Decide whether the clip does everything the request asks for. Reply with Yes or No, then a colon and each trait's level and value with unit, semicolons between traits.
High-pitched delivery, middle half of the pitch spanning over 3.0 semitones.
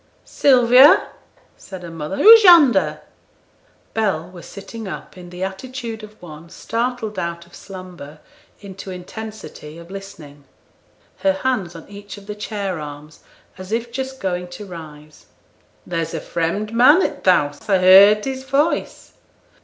Yes: high, 195 Hz; average, 4.9 semitones